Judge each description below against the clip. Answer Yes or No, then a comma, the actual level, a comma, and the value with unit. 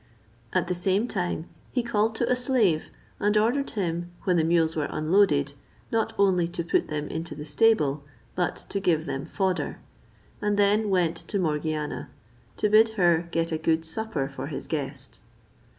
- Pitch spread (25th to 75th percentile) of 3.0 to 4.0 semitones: No, average, 4.6 semitones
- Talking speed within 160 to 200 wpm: Yes, average, 170 wpm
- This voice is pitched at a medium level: Yes, medium, 175 Hz